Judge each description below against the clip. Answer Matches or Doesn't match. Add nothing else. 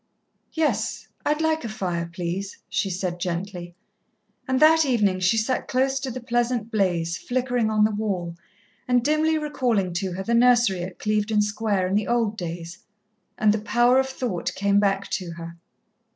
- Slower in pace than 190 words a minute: Matches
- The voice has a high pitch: Matches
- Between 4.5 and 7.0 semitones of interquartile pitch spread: Matches